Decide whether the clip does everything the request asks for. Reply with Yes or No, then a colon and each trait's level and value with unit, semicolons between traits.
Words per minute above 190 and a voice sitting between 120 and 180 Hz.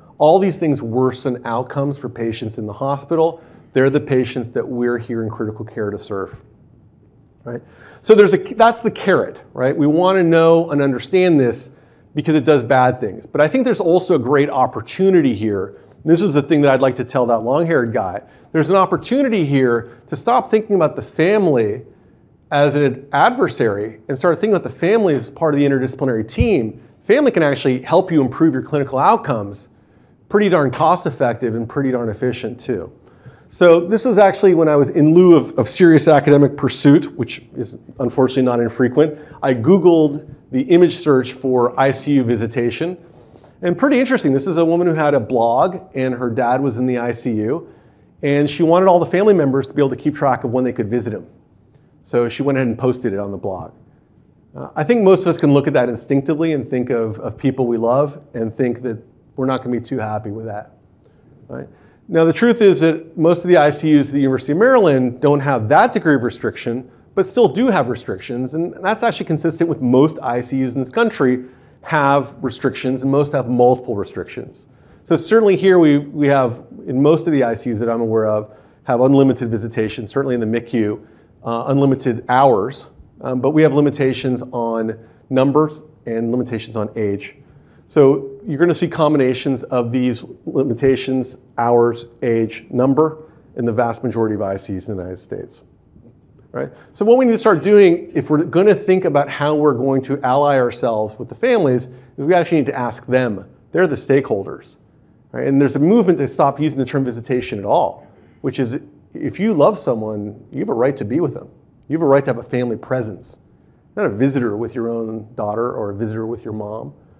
Yes: average, 200 wpm; low, 135 Hz